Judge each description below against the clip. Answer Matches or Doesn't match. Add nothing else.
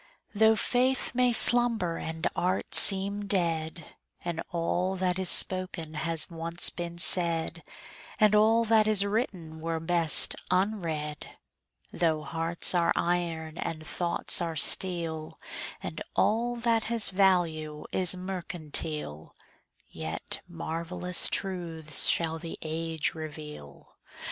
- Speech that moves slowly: Matches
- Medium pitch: Matches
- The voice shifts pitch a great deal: Doesn't match